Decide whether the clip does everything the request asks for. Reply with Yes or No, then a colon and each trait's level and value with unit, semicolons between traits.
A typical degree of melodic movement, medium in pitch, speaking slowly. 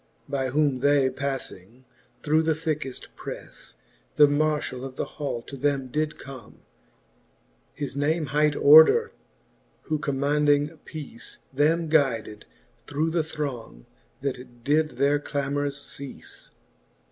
No: narrow, 2.3 semitones; medium, 145 Hz; slow, 120 wpm